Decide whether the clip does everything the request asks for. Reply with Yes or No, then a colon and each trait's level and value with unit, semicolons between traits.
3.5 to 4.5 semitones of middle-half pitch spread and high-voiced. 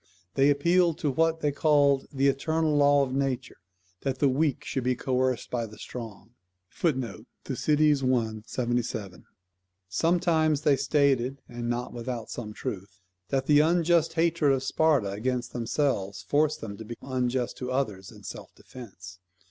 No: average, 3.8 semitones; low, 130 Hz